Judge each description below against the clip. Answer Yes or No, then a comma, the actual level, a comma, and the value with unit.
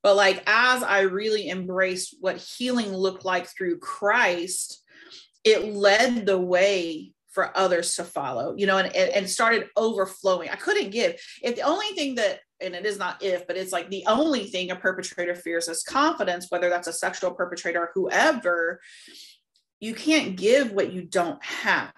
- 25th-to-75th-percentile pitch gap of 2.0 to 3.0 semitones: No, average, 4.0 semitones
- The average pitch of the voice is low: No, high, 190 Hz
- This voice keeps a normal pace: Yes, average, 175 wpm